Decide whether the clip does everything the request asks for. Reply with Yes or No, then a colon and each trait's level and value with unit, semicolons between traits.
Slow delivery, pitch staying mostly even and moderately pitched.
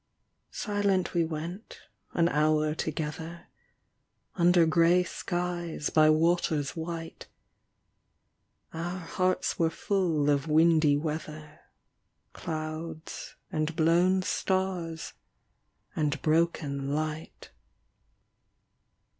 Yes: slow, 80 wpm; narrow, 2.1 semitones; medium, 165 Hz